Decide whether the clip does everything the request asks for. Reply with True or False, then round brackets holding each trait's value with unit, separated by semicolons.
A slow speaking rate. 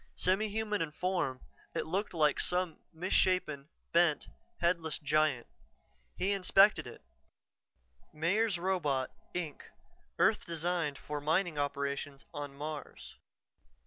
True (110 wpm)